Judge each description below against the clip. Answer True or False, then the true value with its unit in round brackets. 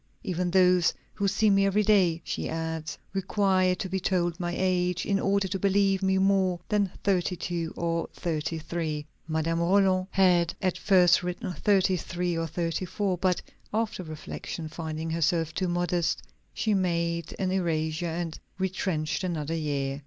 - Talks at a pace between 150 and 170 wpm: True (160 wpm)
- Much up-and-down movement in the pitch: False (2.5 semitones)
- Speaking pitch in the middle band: True (180 Hz)